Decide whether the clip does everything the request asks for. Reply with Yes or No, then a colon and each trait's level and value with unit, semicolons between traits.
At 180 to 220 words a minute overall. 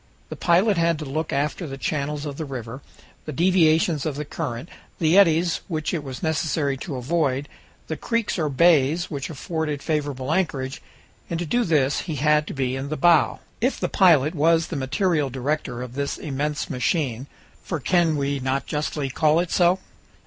Yes: average, 185 wpm